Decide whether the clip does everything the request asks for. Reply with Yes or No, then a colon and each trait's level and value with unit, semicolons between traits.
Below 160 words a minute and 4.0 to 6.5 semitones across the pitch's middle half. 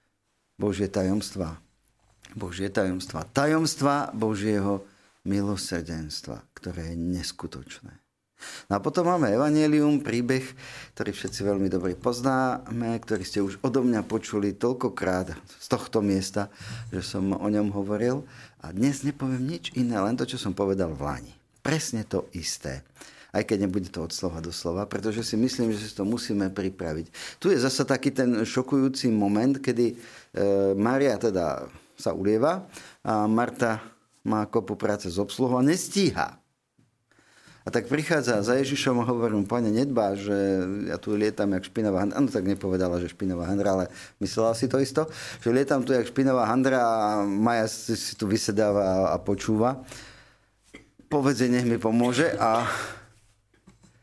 Yes: average, 150 wpm; average, 4.4 semitones